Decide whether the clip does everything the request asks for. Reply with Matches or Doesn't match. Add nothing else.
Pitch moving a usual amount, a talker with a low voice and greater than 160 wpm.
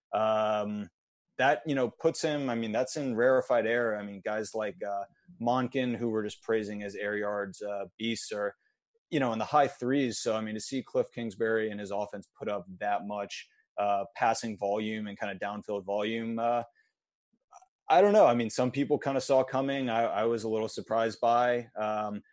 Matches